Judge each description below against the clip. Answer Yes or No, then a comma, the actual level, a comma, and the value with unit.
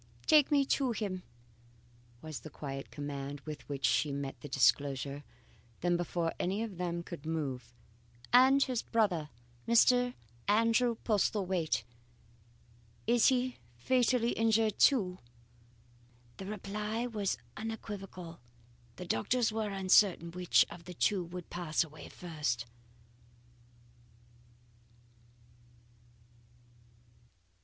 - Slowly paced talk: Yes, slow, 105 wpm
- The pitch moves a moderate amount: No, wide, 6.5 semitones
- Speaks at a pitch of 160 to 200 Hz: Yes, medium, 185 Hz